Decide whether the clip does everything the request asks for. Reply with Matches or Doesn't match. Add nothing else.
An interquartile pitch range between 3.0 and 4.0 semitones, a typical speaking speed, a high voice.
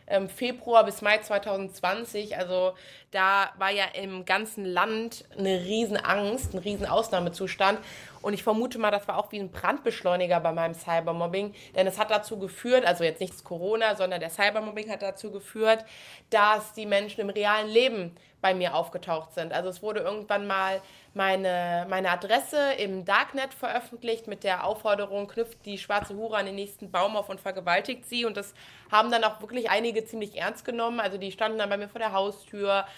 Doesn't match